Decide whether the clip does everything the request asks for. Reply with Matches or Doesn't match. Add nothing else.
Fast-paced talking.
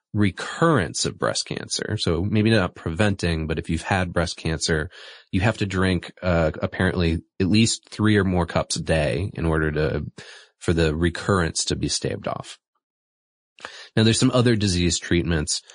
Doesn't match